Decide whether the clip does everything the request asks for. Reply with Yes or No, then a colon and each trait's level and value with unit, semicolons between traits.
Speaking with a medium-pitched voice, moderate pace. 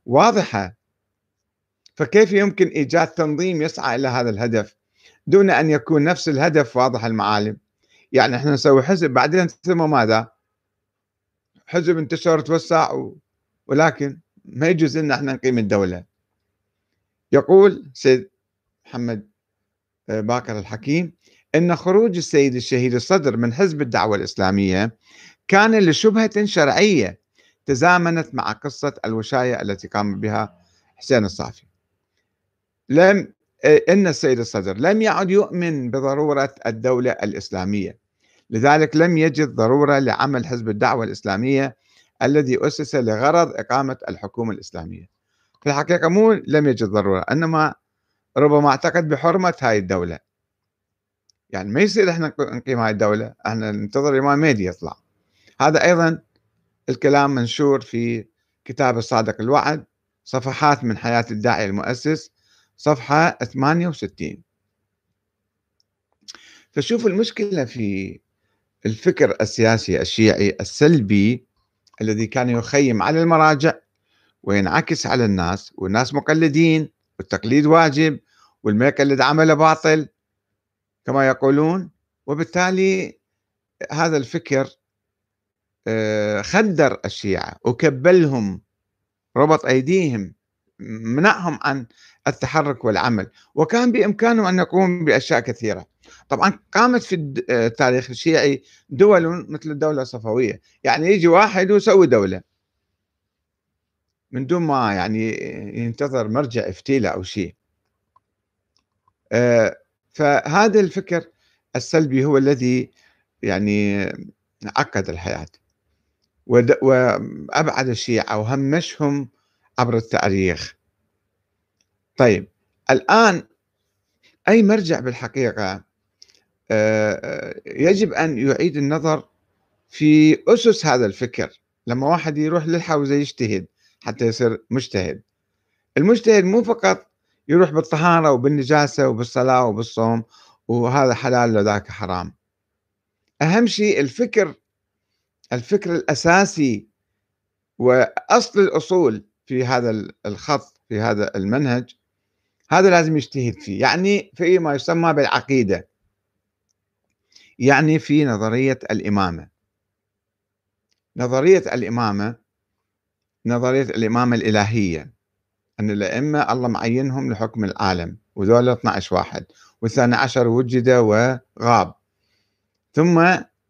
No: low, 125 Hz; average, 95 wpm